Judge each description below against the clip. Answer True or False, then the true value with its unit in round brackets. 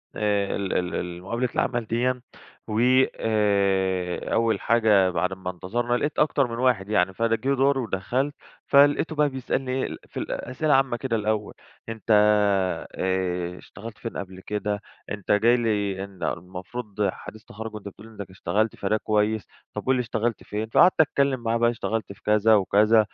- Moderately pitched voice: False (110 Hz)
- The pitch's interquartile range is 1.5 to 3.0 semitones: False (3.6 semitones)